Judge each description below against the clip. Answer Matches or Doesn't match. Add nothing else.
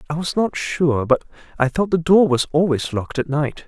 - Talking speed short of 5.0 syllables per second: Doesn't match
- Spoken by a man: Matches